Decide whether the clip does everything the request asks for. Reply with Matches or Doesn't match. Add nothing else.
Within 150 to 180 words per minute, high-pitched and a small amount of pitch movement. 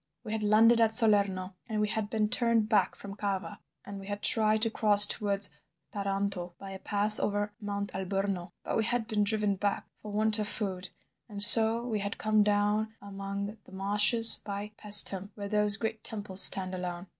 Doesn't match